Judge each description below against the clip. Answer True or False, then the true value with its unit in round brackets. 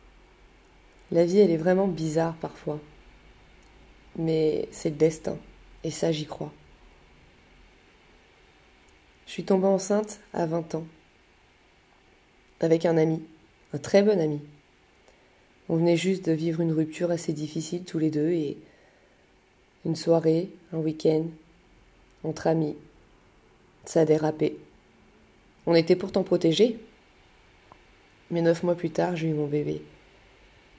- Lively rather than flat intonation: True (7.7 semitones)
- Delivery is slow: True (125 wpm)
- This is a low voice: False (160 Hz)